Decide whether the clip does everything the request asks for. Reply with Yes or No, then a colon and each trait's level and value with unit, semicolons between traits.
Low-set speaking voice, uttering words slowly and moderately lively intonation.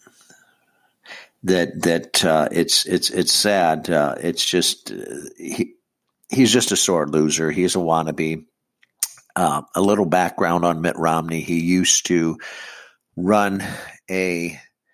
No: very low, 85 Hz; slow, 130 wpm; narrow, 2.1 semitones